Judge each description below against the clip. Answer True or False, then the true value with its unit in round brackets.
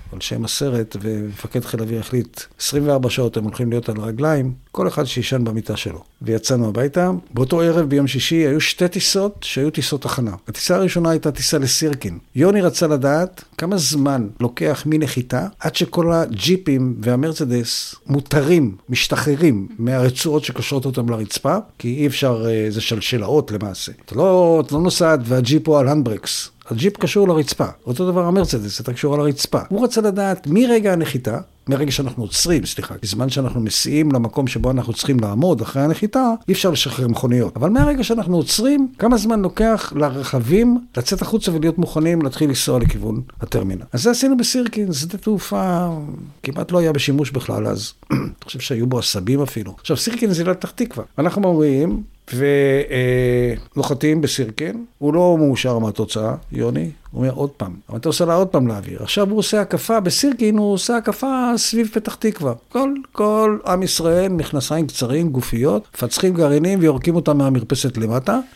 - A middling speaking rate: False (160 wpm)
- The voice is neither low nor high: True (145 Hz)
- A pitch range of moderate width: False (6.5 semitones)